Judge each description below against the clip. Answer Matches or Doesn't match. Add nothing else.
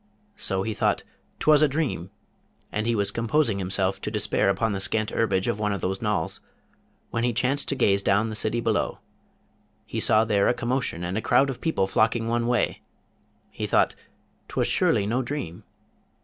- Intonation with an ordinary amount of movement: Matches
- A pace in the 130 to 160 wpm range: Doesn't match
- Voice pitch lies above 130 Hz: Doesn't match